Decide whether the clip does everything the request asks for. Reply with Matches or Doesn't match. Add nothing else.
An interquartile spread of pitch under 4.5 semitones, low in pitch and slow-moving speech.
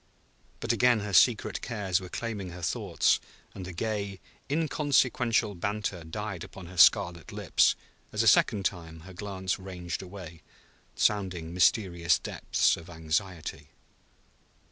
Matches